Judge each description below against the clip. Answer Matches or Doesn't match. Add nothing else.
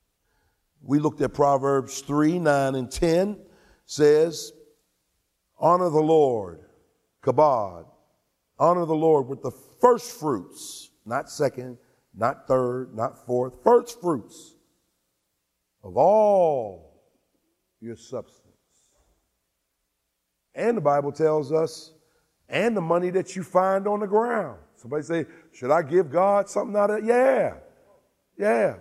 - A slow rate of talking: Matches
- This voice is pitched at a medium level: Matches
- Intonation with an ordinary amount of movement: Doesn't match